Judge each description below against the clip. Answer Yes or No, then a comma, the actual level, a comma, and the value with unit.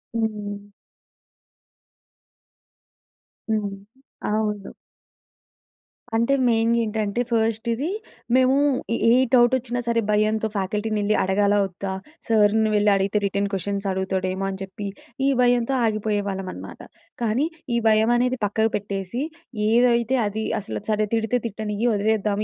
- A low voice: No, high, 215 Hz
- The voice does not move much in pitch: Yes, narrow, 2.2 semitones